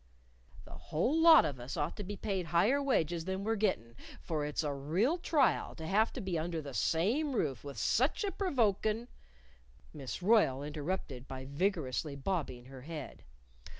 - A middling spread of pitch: No, wide, 7.6 semitones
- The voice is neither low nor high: Yes, medium, 170 Hz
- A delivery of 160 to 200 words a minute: Yes, average, 180 wpm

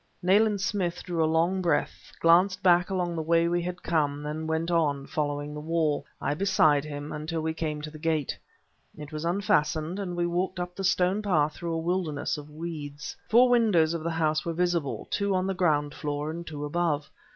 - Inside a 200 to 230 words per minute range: Yes, fast, 205 wpm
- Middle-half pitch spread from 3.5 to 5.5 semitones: No, average, 2.9 semitones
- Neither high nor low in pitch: Yes, medium, 165 Hz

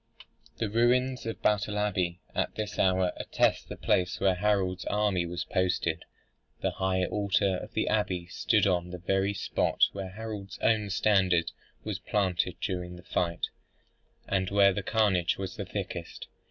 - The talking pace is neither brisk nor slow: Yes, average, 155 wpm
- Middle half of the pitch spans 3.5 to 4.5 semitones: No, narrow, 2.4 semitones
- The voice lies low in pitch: Yes, very low, 95 Hz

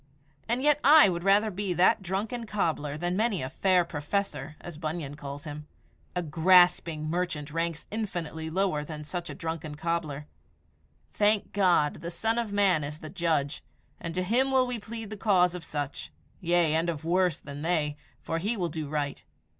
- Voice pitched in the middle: Yes, medium, 170 Hz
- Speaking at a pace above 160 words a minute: Yes, average, 180 wpm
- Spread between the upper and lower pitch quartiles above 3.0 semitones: Yes, average, 4.5 semitones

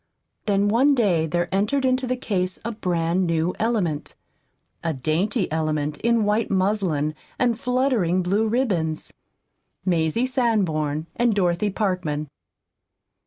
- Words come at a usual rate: No, slow, 120 wpm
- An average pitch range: No, wide, 5.9 semitones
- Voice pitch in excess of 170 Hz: Yes, high, 190 Hz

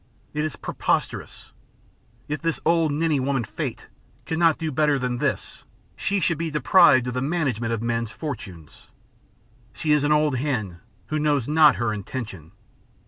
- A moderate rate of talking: Yes, average, 155 wpm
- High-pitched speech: No, medium, 145 Hz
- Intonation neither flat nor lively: Yes, average, 4.6 semitones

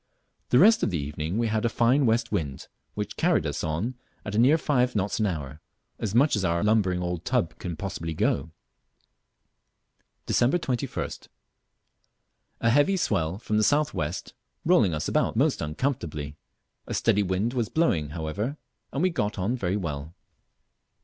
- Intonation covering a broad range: Yes, wide, 6.9 semitones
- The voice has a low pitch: Yes, low, 105 Hz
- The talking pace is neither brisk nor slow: Yes, average, 165 wpm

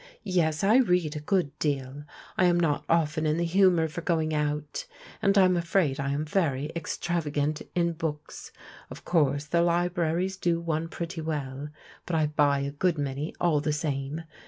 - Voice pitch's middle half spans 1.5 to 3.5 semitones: Yes, average, 2.7 semitones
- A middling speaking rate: Yes, average, 180 wpm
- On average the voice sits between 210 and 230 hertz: No, medium, 160 Hz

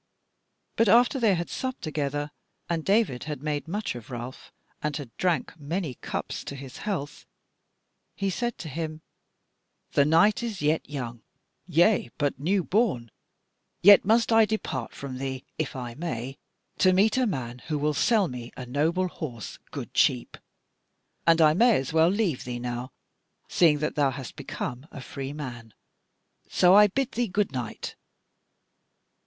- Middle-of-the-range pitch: Yes, medium, 155 Hz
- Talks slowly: No, average, 155 wpm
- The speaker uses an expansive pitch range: Yes, wide, 6.8 semitones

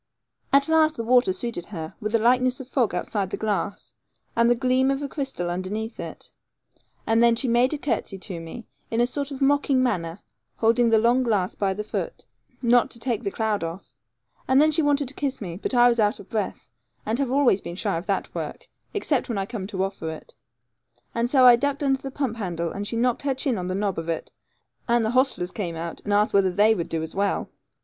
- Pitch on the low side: No, high, 230 Hz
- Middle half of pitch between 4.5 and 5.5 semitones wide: Yes, average, 4.9 semitones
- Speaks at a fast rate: Yes, fast, 235 wpm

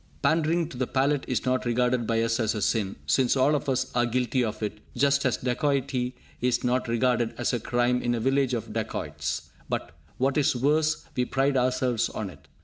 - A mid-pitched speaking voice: No, low, 125 Hz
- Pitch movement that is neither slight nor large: No, narrow, 2.1 semitones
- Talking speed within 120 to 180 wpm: No, fast, 205 wpm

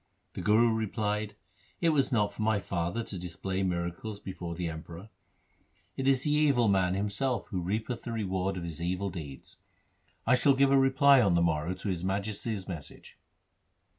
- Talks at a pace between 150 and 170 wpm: No, average, 195 wpm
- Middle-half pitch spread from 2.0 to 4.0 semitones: No, average, 4.6 semitones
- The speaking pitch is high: No, low, 100 Hz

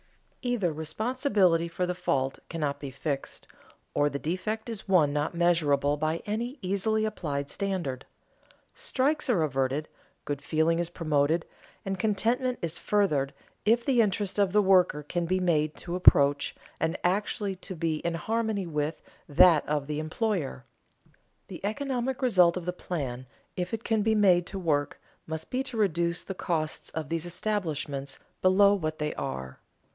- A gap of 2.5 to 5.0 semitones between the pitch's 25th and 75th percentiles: No, wide, 5.4 semitones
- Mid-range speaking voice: Yes, medium, 175 Hz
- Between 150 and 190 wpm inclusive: Yes, average, 160 wpm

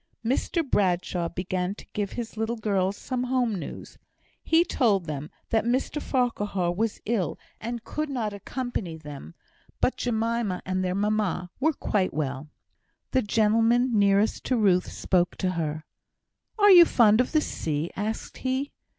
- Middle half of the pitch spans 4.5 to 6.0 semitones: Yes, average, 5.1 semitones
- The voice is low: No, high, 210 Hz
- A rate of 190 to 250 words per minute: No, average, 150 wpm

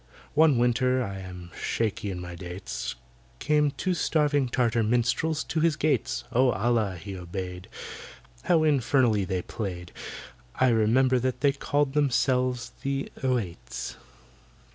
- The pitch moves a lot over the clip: Yes, wide, 6.1 semitones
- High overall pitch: No, low, 125 Hz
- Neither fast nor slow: No, slow, 125 wpm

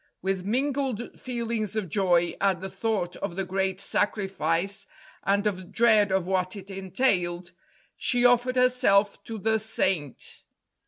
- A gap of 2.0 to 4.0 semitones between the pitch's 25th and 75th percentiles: Yes, average, 3.3 semitones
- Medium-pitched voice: No, high, 200 Hz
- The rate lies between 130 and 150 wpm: Yes, average, 140 wpm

